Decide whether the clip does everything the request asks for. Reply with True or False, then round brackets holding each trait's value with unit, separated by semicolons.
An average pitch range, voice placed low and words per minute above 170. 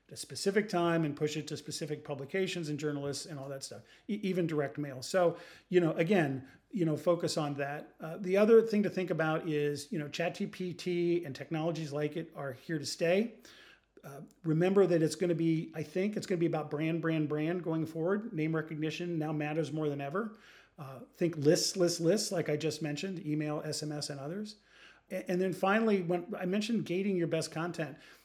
False (3.4 semitones; 165 Hz; 200 wpm)